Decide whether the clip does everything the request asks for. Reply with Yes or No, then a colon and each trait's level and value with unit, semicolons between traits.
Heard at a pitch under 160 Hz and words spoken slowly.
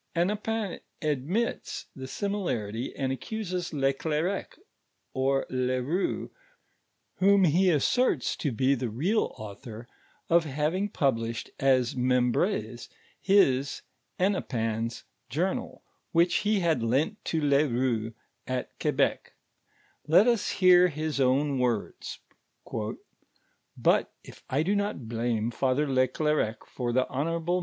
Yes: medium, 140 Hz; slow, 115 wpm